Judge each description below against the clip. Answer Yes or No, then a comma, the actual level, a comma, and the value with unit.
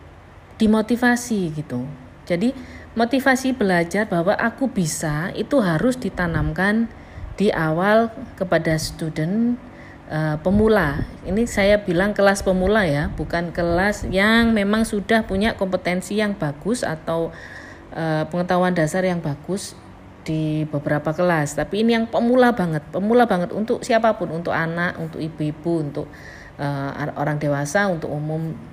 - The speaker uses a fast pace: No, average, 125 wpm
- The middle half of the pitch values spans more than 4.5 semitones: Yes, wide, 5.5 semitones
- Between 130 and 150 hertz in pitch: No, medium, 180 Hz